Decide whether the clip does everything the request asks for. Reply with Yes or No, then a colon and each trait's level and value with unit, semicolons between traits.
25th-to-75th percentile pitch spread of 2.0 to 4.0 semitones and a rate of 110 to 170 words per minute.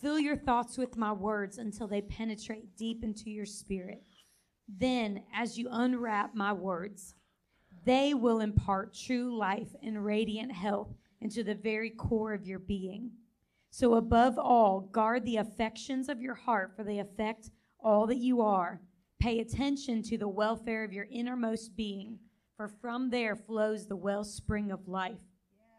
Yes: narrow, 2.4 semitones; average, 155 wpm